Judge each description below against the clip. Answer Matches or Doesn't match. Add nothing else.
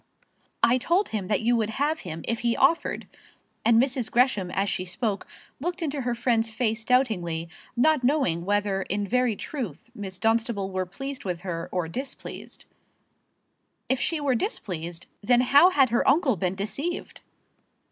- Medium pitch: Doesn't match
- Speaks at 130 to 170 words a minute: Matches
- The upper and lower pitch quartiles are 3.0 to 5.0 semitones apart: Doesn't match